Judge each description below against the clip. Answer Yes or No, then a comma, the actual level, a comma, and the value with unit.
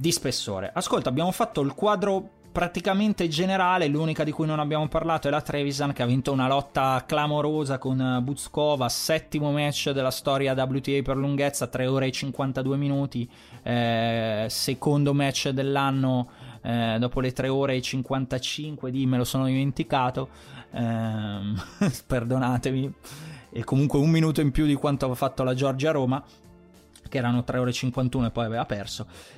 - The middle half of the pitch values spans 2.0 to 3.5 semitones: Yes, average, 2.8 semitones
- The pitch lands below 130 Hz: No, low, 135 Hz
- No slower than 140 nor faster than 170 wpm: Yes, average, 165 wpm